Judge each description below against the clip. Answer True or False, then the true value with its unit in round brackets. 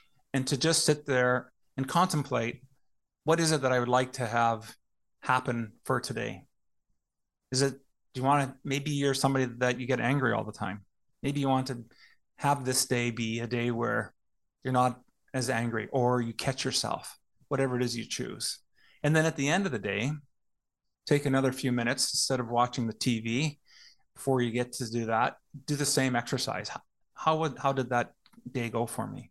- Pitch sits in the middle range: False (130 Hz)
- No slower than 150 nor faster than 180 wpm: False (195 wpm)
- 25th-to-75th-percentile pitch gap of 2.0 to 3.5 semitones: True (2.5 semitones)